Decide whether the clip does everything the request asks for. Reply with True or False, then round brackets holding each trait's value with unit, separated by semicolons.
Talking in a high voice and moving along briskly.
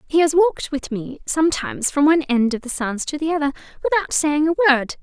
True (285 Hz; 225 wpm)